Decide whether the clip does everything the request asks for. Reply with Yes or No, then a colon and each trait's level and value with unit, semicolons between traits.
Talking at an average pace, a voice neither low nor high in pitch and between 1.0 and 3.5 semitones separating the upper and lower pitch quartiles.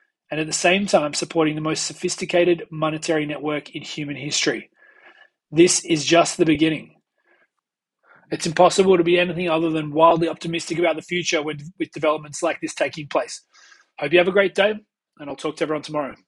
Yes: average, 185 wpm; medium, 165 Hz; narrow, 2.5 semitones